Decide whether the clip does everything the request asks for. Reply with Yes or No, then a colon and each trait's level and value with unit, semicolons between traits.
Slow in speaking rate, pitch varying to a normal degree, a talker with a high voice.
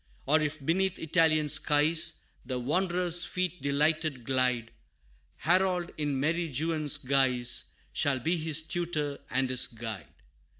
No: slow, 125 wpm; average, 4.0 semitones; medium, 150 Hz